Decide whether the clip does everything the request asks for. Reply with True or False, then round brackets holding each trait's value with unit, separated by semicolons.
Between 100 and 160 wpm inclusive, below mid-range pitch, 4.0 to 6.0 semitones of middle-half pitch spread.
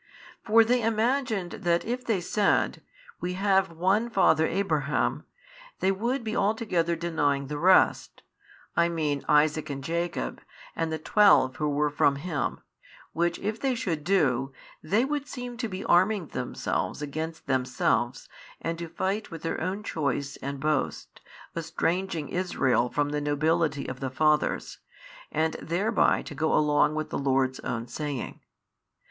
False (150 wpm; 165 Hz; 5.1 semitones)